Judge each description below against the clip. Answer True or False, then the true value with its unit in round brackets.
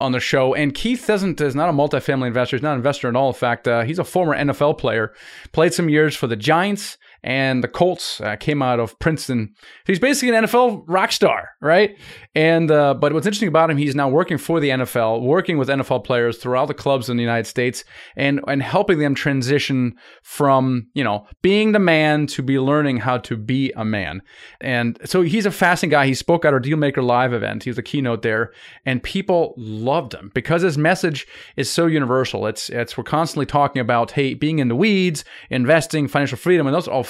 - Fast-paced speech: True (220 wpm)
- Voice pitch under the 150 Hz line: True (140 Hz)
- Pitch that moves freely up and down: False (4.5 semitones)